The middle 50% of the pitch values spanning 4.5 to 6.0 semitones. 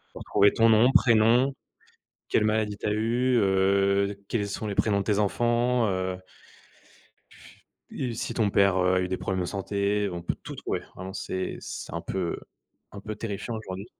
No: average, 2.7 semitones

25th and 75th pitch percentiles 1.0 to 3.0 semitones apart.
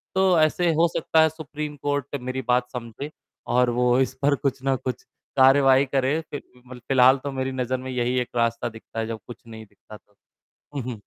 Yes: narrow, 2.6 semitones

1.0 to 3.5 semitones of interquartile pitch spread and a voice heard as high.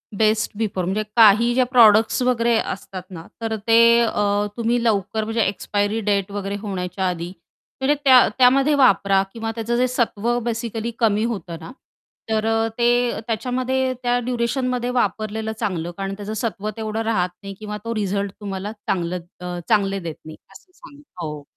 Yes: average, 3.1 semitones; high, 220 Hz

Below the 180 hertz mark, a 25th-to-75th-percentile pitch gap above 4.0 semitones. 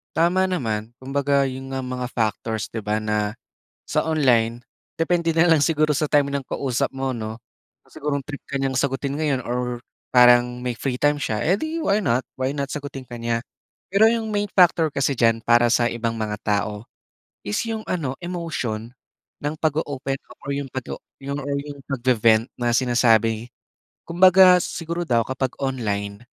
Yes: low, 135 Hz; average, 4.4 semitones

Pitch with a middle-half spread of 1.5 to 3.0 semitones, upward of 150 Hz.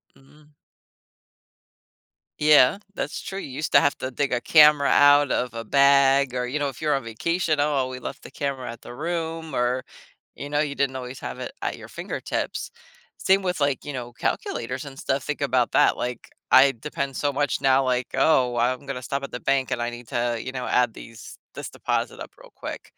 No: narrow, 2.6 semitones; low, 135 Hz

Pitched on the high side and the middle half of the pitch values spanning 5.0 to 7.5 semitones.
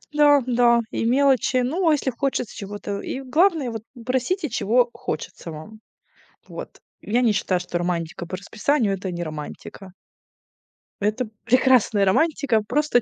Yes: high, 235 Hz; wide, 5.5 semitones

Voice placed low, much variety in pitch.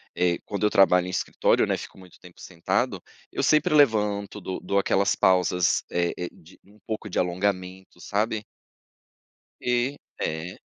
No: very low, 95 Hz; average, 2.8 semitones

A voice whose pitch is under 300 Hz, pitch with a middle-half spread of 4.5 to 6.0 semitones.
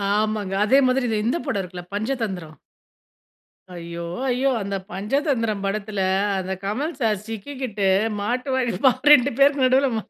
Yes: high, 225 Hz; average, 4.9 semitones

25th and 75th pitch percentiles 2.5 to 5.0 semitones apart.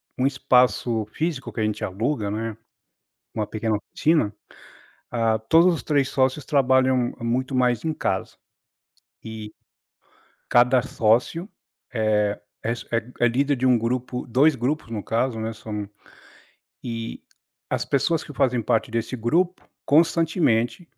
Yes: average, 3.7 semitones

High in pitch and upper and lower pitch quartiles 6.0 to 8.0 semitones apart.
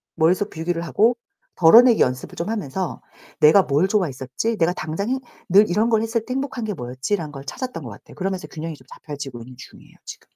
No: medium, 175 Hz; wide, 6.8 semitones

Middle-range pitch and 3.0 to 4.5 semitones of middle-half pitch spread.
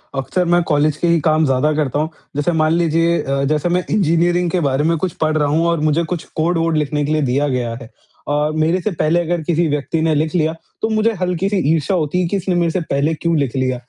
No: medium, 160 Hz; narrow, 2.6 semitones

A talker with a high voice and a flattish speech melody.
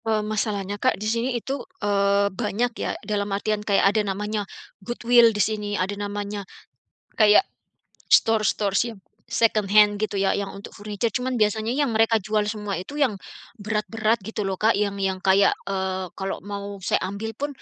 Yes: high, 210 Hz; narrow, 1.8 semitones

